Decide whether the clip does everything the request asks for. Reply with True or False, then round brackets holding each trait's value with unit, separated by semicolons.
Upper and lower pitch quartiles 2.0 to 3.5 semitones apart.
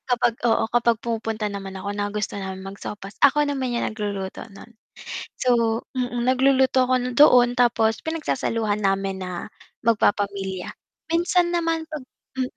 False (4.2 semitones)